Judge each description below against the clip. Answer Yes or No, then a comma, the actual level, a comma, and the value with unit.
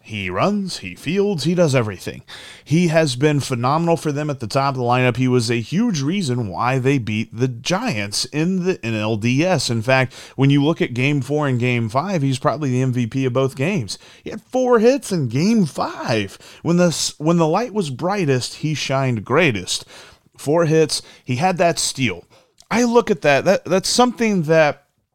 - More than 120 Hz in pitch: Yes, medium, 140 Hz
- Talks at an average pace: Yes, average, 195 wpm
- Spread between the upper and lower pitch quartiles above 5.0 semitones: Yes, wide, 5.6 semitones